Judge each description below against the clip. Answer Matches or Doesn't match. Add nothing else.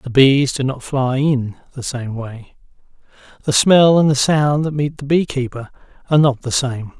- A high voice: Doesn't match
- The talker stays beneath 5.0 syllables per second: Matches